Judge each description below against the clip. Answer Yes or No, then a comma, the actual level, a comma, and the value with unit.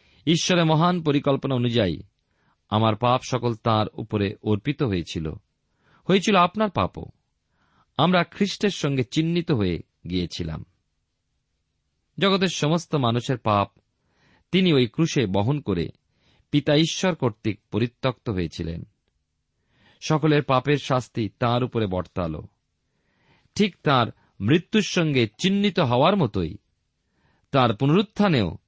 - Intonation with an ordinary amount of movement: No, wide, 7.7 semitones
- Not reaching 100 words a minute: No, average, 105 wpm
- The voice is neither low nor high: No, low, 125 Hz